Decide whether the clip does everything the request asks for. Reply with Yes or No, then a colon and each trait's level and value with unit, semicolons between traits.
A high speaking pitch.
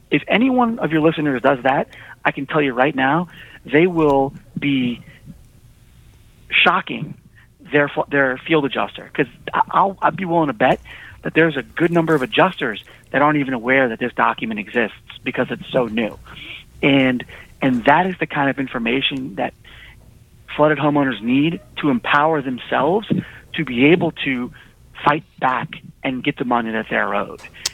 No: medium, 140 Hz